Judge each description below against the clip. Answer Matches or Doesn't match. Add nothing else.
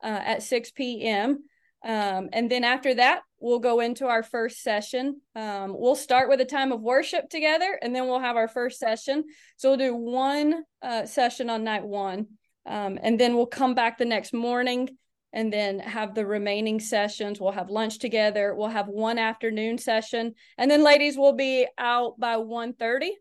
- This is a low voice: Doesn't match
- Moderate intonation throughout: Matches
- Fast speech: Doesn't match